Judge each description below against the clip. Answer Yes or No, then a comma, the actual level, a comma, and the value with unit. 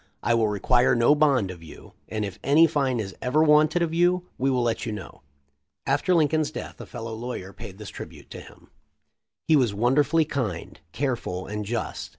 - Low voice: Yes, low, 125 Hz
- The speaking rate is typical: Yes, average, 195 wpm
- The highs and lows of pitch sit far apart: Yes, wide, 5.9 semitones